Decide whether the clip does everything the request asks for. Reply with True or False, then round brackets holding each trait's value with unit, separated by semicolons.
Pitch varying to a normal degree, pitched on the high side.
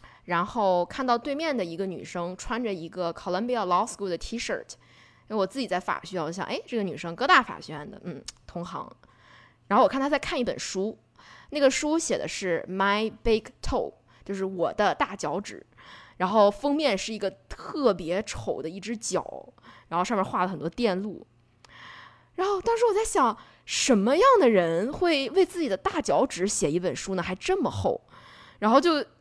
False (6.9 semitones; 205 Hz)